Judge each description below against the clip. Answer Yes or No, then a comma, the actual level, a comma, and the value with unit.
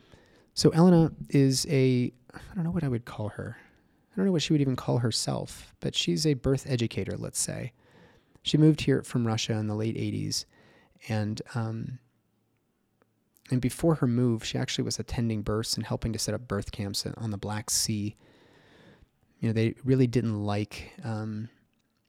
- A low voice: Yes, low, 120 Hz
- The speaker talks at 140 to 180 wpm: Yes, average, 175 wpm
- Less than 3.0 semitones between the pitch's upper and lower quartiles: No, average, 3.8 semitones